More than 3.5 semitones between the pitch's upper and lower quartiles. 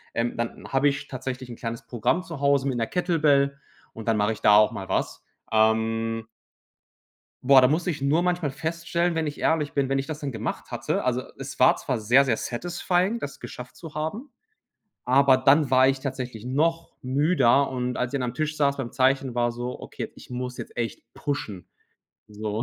Yes: average, 3.9 semitones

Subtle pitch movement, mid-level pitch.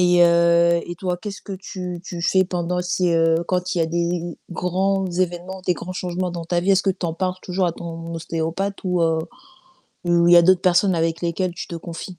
Yes: narrow, 1.4 semitones; medium, 175 Hz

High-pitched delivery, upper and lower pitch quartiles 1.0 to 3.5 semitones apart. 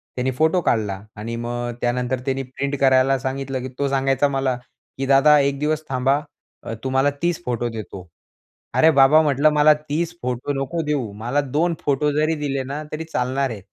No: low, 135 Hz; average, 2.8 semitones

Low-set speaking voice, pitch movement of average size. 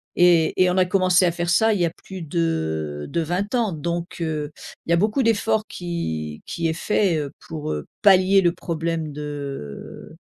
No: medium, 170 Hz; average, 3.6 semitones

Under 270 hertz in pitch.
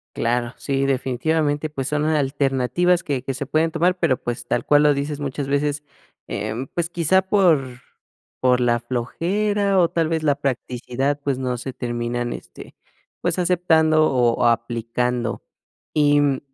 Yes: medium, 140 Hz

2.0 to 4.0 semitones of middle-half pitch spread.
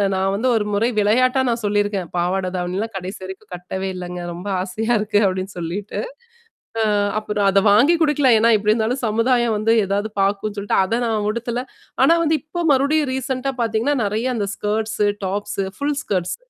Yes: average, 3.5 semitones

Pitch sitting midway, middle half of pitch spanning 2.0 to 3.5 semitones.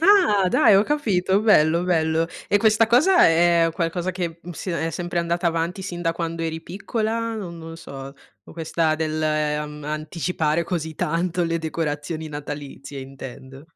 Yes: medium, 165 Hz; average, 2.7 semitones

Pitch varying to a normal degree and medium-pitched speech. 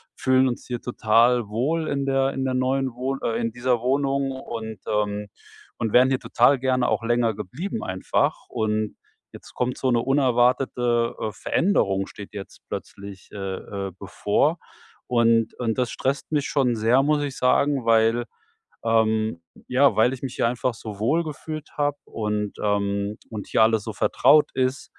No: average, 3.4 semitones; low, 120 Hz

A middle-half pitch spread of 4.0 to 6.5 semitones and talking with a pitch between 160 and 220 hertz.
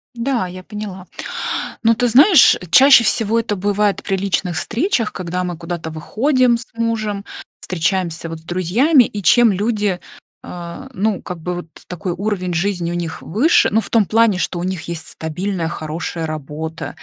Yes: average, 4.7 semitones; high, 190 Hz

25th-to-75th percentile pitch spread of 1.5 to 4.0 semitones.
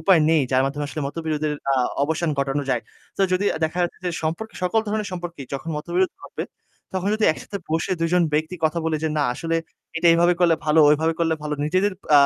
Yes: average, 2.8 semitones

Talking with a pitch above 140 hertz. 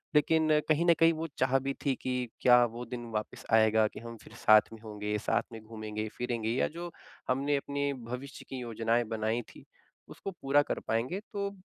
No: low, 125 Hz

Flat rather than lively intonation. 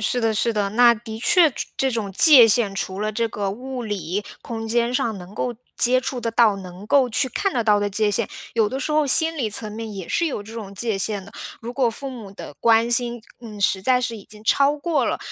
No: average, 3.3 semitones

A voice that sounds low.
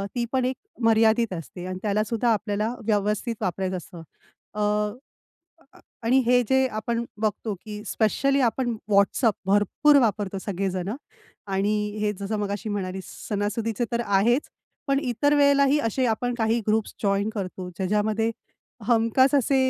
No: high, 215 Hz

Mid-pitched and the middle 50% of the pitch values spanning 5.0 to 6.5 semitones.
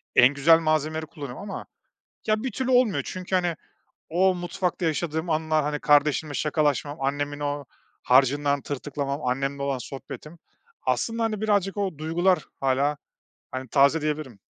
No: medium, 150 Hz; average, 3.8 semitones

